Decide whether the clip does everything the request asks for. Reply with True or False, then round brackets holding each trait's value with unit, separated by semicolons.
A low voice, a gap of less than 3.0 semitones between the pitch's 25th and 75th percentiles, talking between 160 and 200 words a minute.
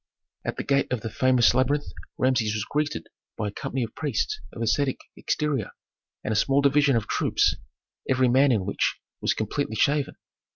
False (130 Hz; 4.2 semitones; 175 wpm)